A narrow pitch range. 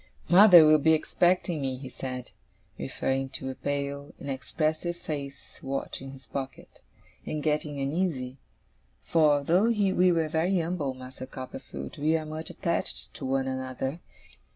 No: average, 3.5 semitones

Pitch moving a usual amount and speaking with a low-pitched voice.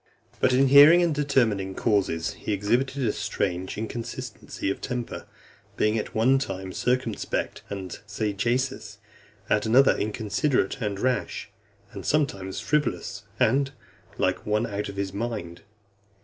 Yes: average, 4.7 semitones; low, 110 Hz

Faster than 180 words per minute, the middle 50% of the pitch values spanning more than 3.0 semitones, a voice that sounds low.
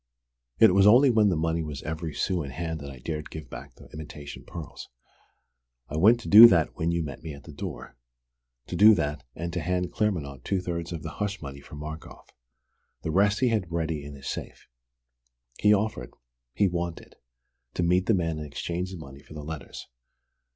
Yes: average, 200 wpm; average, 3.7 semitones; very low, 85 Hz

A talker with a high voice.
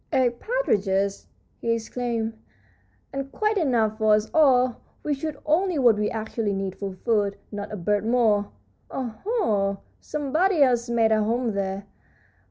Yes: high, 230 Hz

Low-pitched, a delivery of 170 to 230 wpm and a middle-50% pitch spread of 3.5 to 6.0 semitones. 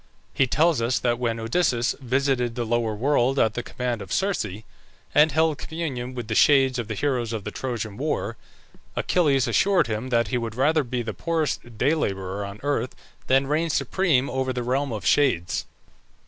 Yes: low, 125 Hz; average, 185 wpm; average, 3.9 semitones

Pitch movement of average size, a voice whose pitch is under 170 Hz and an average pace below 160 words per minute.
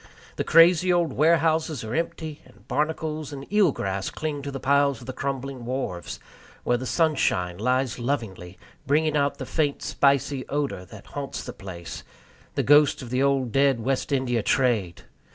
No: average, 3.8 semitones; medium, 140 Hz; average, 170 wpm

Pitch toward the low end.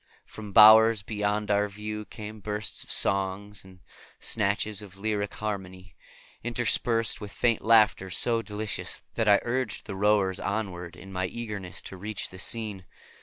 Yes: low, 105 Hz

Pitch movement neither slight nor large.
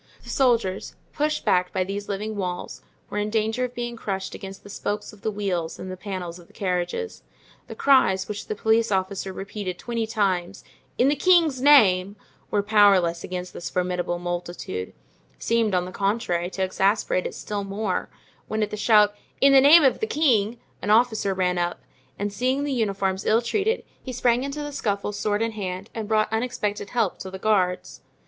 Yes: average, 3.8 semitones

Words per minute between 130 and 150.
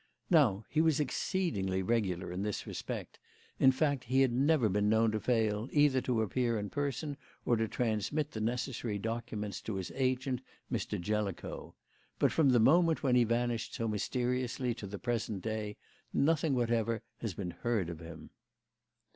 No: average, 165 wpm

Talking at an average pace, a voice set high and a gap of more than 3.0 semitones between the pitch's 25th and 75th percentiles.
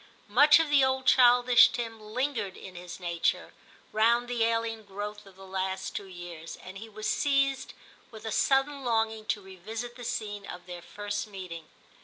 Yes: average, 175 wpm; high, 220 Hz; average, 4.2 semitones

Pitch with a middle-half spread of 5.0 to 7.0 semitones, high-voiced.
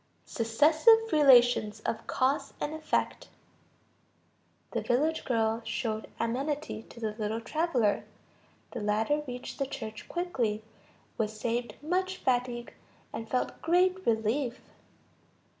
Yes: wide, 5.4 semitones; high, 245 Hz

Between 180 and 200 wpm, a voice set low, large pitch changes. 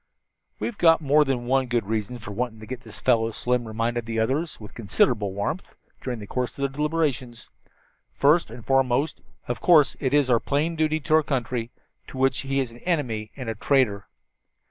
No: average, 190 wpm; low, 125 Hz; average, 3.8 semitones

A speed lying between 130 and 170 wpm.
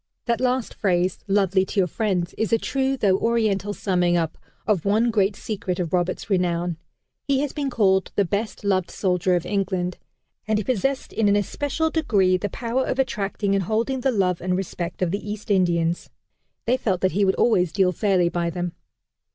No: average, 190 wpm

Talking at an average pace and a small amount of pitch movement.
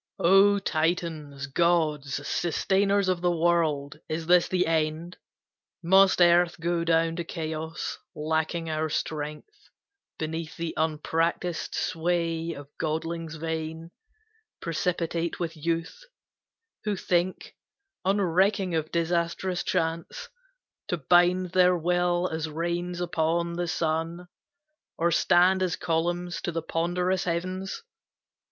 No: slow, 110 wpm; narrow, 1.7 semitones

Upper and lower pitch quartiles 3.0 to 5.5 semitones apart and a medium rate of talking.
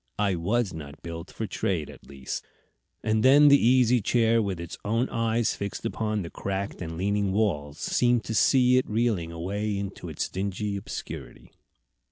Yes: average, 4.1 semitones; average, 170 wpm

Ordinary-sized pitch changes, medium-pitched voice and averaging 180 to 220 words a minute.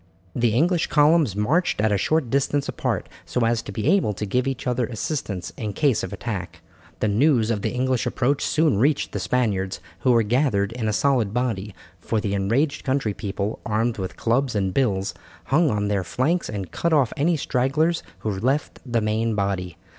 No: average, 4.9 semitones; low, 120 Hz; average, 190 wpm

